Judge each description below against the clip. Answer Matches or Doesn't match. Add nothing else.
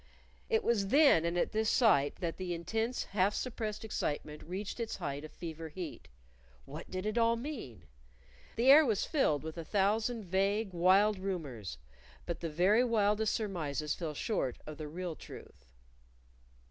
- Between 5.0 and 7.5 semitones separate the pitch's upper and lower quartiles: Matches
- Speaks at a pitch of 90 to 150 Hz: Doesn't match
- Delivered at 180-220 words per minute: Doesn't match